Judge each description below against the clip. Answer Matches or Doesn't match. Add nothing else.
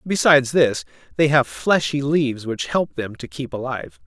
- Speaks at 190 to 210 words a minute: Doesn't match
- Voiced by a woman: Doesn't match